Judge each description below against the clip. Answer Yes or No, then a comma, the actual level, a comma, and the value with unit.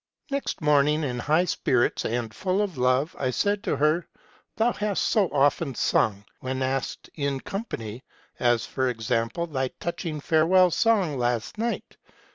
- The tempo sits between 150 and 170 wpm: Yes, average, 155 wpm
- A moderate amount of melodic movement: No, wide, 6.1 semitones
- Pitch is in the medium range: Yes, medium, 145 Hz